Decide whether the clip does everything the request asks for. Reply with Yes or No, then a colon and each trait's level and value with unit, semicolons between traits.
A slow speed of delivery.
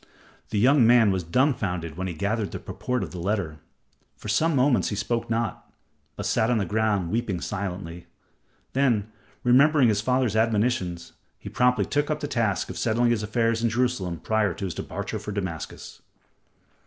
No: average, 175 wpm